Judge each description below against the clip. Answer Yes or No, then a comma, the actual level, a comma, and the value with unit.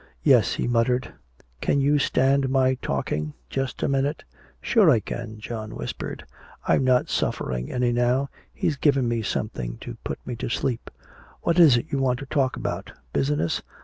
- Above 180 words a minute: No, average, 170 wpm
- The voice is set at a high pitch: No, low, 125 Hz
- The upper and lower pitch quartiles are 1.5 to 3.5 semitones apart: Yes, average, 3.1 semitones